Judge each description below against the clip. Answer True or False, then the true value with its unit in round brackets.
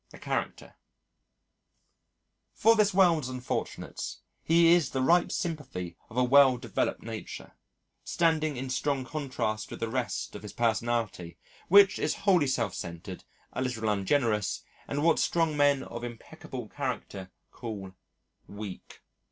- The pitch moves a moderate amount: False (5.9 semitones)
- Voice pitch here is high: False (130 Hz)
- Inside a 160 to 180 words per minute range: False (135 wpm)